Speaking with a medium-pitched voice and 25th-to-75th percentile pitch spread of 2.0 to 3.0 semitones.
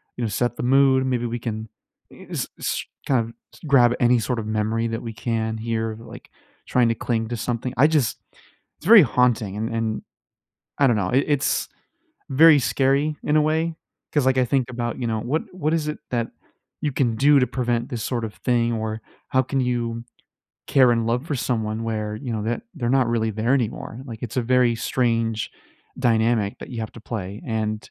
No: low, 120 Hz; average, 2.7 semitones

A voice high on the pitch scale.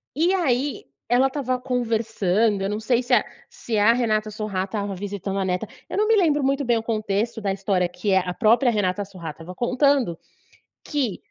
Yes: high, 220 Hz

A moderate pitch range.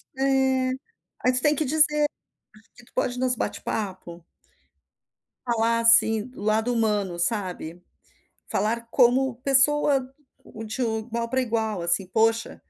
Yes: average, 3.1 semitones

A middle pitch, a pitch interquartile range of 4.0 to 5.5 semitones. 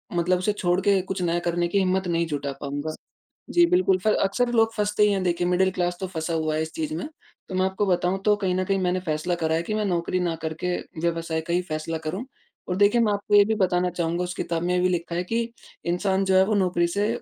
No: medium, 180 Hz; average, 2.8 semitones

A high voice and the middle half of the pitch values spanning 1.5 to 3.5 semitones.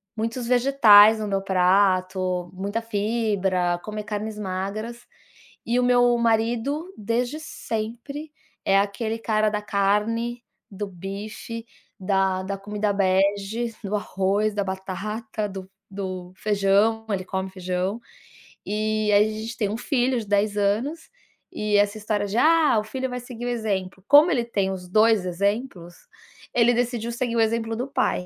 Yes: high, 210 Hz; average, 2.9 semitones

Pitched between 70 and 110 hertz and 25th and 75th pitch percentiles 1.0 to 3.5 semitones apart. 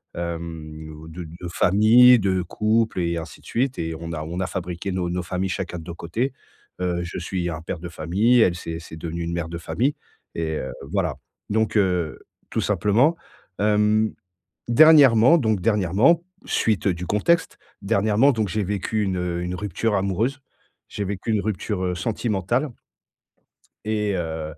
No: very low, 95 Hz; average, 4.3 semitones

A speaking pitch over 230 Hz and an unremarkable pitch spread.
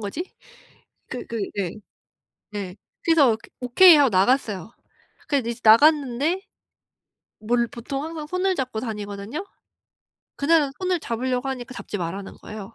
No: very high, 250 Hz; wide, 5.8 semitones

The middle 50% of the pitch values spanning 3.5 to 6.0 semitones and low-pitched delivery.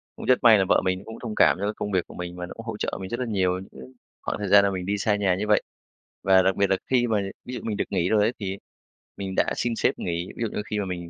No: average, 2.8 semitones; low, 100 Hz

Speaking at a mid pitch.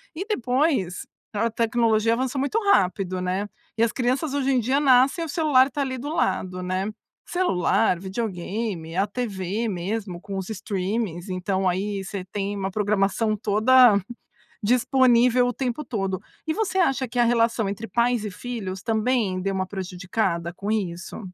No: high, 215 Hz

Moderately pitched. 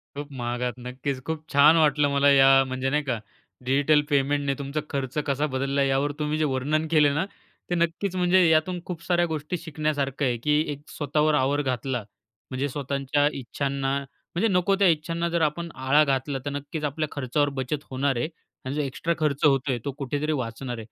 Yes: medium, 145 Hz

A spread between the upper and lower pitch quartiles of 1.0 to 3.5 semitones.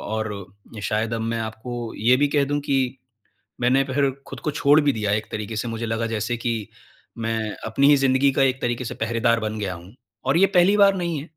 No: average, 3.9 semitones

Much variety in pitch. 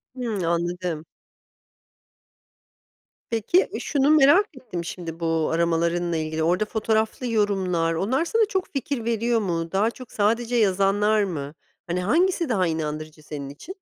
Yes: wide, 6.0 semitones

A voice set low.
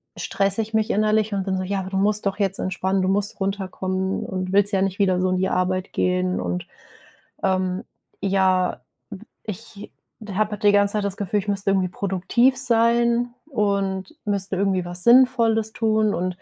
No: high, 195 Hz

